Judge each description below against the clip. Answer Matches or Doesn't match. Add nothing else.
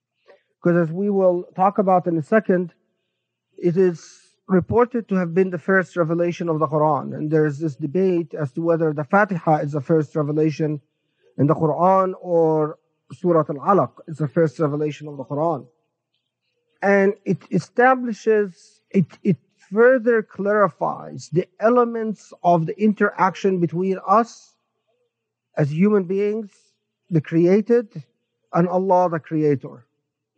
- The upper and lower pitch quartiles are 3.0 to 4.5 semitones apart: Matches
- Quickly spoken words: Doesn't match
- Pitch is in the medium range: Matches